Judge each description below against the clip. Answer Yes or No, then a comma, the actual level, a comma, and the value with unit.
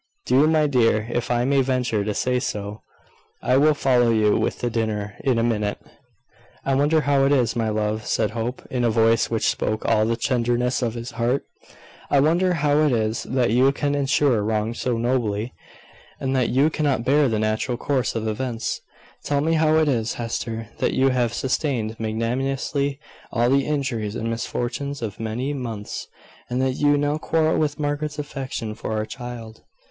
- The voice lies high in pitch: No, low, 125 Hz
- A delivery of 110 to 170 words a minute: No, average, 185 wpm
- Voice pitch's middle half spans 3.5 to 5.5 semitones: Yes, average, 3.8 semitones